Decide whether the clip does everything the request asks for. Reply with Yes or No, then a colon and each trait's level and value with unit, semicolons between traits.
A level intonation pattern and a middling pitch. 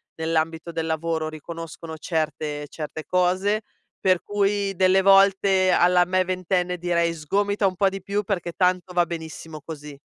No: average, 3.0 semitones; medium, 175 Hz